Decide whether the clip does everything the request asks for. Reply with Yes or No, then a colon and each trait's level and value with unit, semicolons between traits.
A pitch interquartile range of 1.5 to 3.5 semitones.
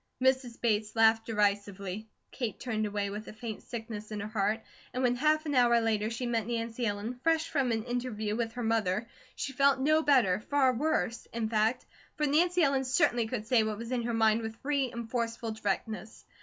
Yes: average, 2.9 semitones